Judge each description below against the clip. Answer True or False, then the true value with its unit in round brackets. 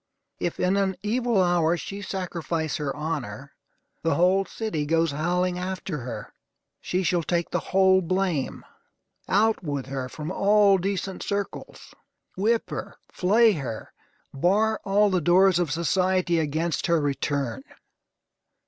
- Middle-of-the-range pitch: True (180 Hz)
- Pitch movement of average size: True (3.8 semitones)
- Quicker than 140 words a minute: False (135 wpm)